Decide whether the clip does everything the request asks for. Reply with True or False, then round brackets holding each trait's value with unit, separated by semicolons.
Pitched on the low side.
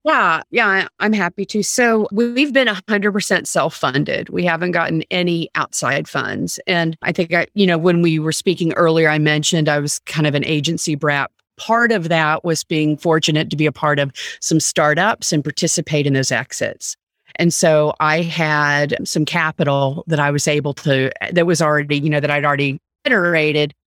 False (160 Hz)